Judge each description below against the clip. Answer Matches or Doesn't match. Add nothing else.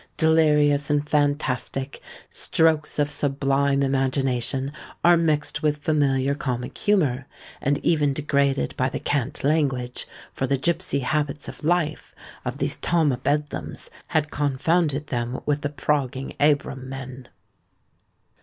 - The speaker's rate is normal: Doesn't match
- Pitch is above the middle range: Doesn't match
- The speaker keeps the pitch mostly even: Matches